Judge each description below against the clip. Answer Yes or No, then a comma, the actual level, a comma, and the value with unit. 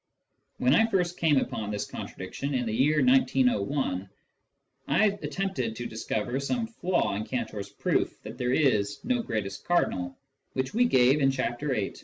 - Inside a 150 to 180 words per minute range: Yes, average, 160 wpm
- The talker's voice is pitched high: No, low, 135 Hz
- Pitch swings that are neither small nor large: No, wide, 8.3 semitones